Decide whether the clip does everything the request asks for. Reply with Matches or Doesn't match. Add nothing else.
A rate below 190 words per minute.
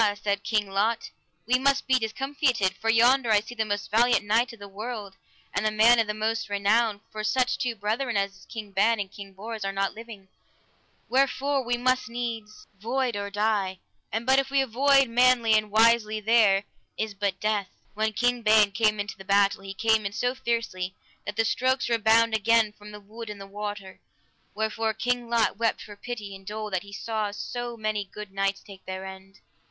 Doesn't match